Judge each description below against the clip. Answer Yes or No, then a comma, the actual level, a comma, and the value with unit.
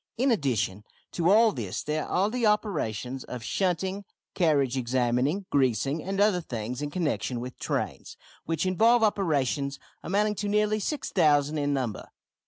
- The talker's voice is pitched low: No, medium, 155 Hz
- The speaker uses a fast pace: No, average, 145 wpm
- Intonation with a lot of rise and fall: Yes, wide, 7.6 semitones